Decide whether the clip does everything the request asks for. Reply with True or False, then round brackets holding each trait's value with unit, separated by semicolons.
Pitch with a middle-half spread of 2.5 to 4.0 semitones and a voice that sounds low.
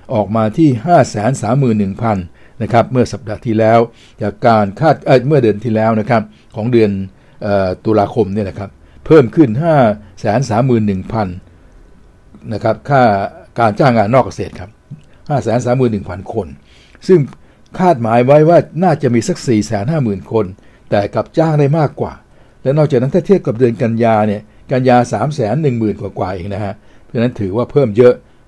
True (3.7 semitones; 115 Hz)